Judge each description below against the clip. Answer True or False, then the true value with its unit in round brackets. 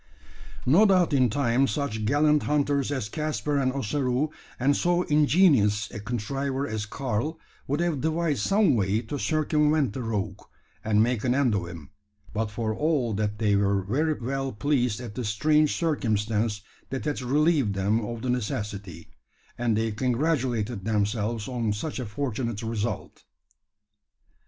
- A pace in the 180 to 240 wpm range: False (150 wpm)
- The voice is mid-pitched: False (125 Hz)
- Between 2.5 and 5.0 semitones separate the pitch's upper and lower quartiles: False (5.4 semitones)